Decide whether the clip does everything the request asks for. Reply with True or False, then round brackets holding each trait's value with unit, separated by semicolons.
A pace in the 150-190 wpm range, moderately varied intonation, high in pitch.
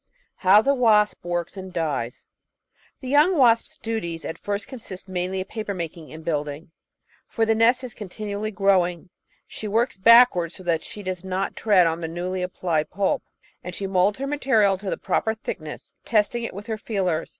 True (185 wpm; 4.1 semitones; 195 Hz)